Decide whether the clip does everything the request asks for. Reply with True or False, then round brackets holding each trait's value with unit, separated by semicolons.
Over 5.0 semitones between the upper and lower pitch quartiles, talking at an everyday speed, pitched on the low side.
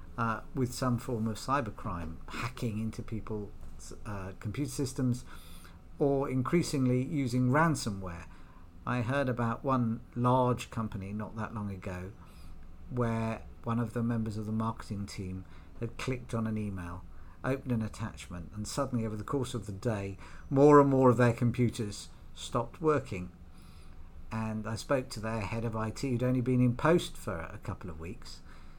True (5.6 semitones; 160 wpm; 110 Hz)